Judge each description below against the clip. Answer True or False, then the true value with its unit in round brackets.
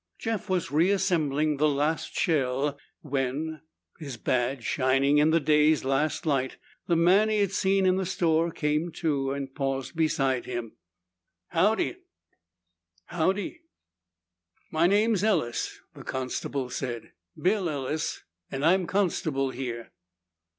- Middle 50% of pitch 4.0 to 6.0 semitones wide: True (4.7 semitones)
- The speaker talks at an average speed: False (120 wpm)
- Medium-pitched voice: True (155 Hz)